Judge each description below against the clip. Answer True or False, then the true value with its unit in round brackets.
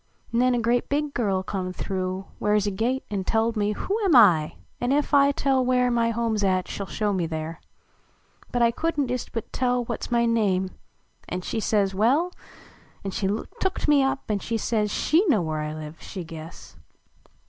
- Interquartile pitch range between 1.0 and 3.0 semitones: False (4.9 semitones)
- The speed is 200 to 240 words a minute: True (205 wpm)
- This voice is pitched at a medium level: False (225 Hz)